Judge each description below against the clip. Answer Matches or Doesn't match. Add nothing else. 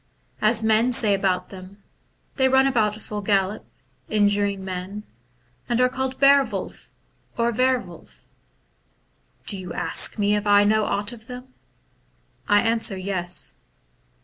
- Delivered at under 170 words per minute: Matches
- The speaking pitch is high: Matches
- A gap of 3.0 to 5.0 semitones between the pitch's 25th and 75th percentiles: Matches